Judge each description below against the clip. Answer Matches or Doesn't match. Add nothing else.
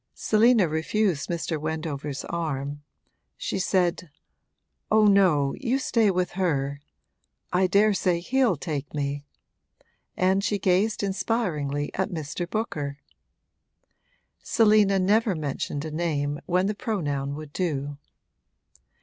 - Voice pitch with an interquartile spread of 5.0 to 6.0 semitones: Matches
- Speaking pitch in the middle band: Matches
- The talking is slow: Matches